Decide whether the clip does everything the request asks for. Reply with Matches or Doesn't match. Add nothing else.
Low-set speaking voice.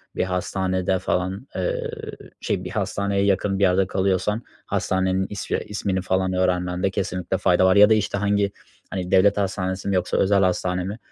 Matches